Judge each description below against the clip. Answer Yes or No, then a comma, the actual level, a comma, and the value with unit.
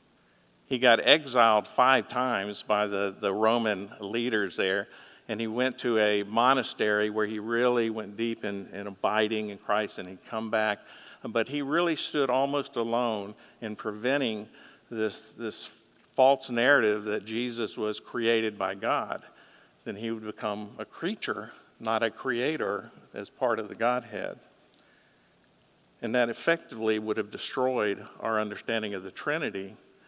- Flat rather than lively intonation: Yes, narrow, 2.3 semitones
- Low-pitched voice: Yes, low, 110 Hz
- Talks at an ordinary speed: Yes, average, 150 wpm